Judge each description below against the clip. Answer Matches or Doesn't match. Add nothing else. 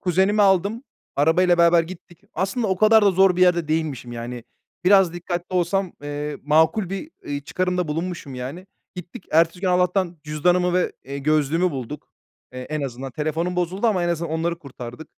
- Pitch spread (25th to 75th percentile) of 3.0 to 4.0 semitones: Matches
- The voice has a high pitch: Doesn't match